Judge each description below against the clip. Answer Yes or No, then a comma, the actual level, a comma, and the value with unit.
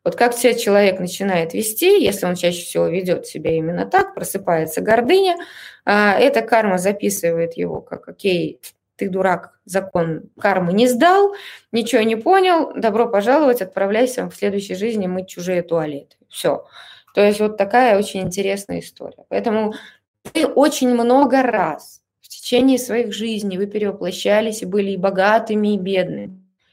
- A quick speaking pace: No, average, 145 wpm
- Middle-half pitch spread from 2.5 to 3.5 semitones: No, average, 4.2 semitones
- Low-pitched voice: No, high, 205 Hz